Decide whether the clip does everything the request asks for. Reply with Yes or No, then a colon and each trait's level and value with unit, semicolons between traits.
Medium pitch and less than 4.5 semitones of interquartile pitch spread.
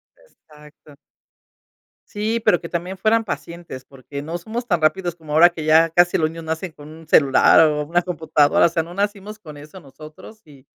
Yes: medium, 165 Hz; average, 3.4 semitones